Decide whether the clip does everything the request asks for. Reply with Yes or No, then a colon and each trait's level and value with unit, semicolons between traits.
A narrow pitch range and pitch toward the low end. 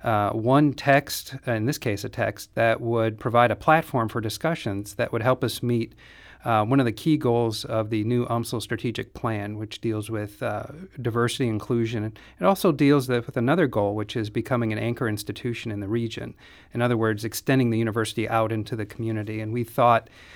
Yes: narrow, 2.2 semitones; low, 115 Hz